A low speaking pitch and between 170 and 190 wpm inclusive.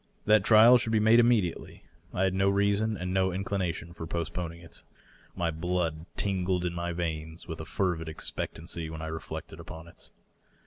Yes: very low, 90 Hz; average, 180 wpm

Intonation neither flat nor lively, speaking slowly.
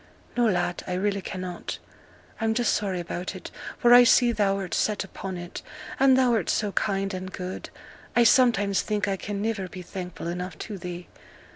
No: average, 3.3 semitones; average, 175 wpm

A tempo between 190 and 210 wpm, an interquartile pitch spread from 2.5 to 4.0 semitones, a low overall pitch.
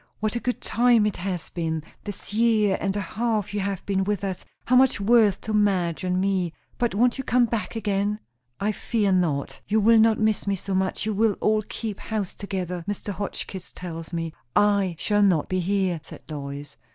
No: average, 200 wpm; average, 2.9 semitones; high, 200 Hz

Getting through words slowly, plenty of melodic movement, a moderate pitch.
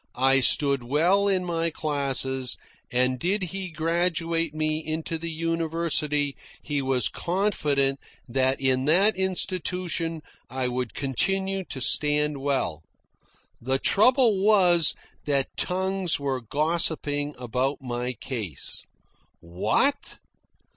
No: slow, 110 wpm; average, 4.8 semitones; medium, 150 Hz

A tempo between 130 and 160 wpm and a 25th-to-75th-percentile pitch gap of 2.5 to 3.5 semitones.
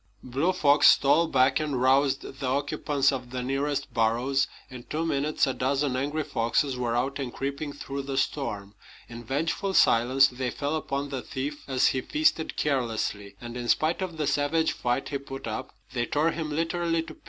No: average, 190 wpm; average, 2.8 semitones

